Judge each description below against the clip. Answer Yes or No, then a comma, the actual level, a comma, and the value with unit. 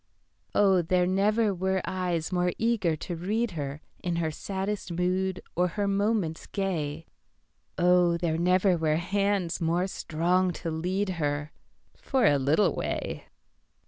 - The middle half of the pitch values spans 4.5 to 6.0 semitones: No, average, 3.0 semitones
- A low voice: No, medium, 180 Hz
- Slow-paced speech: Yes, slow, 125 wpm